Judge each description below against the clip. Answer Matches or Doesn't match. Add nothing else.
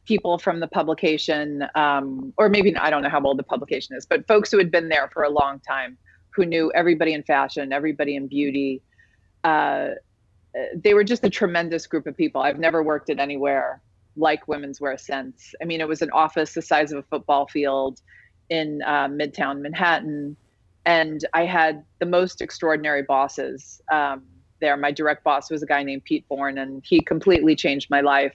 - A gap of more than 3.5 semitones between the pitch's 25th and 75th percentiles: Doesn't match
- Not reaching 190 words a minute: Doesn't match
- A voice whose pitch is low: Doesn't match